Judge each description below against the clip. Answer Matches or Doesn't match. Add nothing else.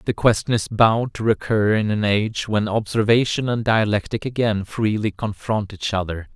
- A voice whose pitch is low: Matches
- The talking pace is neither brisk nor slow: Matches